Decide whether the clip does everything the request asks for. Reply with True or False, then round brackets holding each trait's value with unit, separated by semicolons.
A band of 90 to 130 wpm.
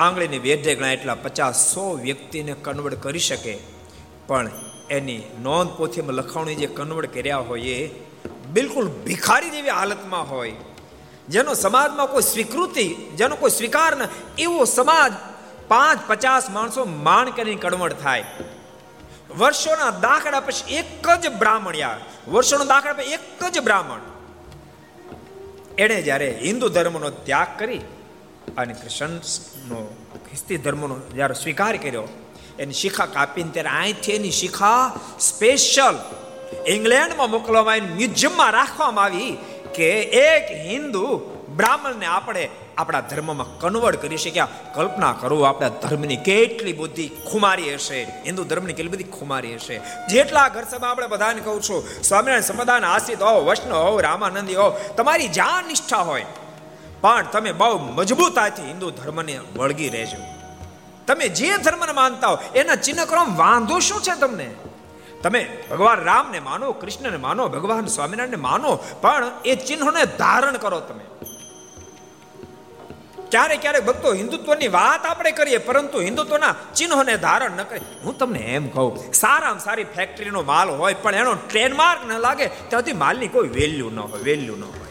False (140 wpm)